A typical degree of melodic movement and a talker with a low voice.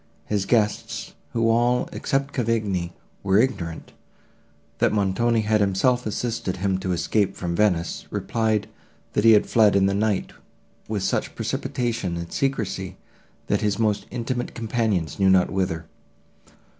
Yes: average, 3.4 semitones; low, 105 Hz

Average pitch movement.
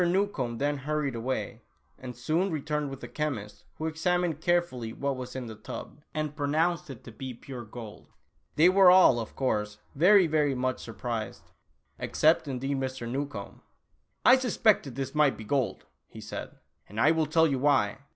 Yes: average, 4.4 semitones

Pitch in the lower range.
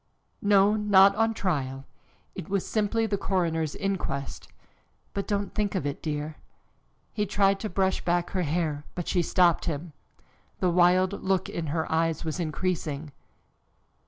No: medium, 180 Hz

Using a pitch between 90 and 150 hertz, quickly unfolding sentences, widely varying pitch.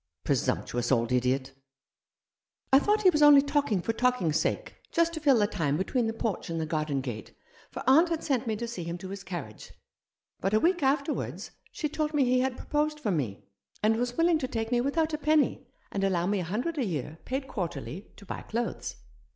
No: high, 230 Hz; fast, 225 wpm; wide, 9.0 semitones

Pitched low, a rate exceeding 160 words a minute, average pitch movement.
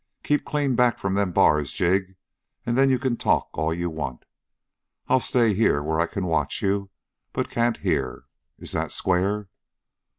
No: very low, 95 Hz; average, 170 wpm; wide, 5.7 semitones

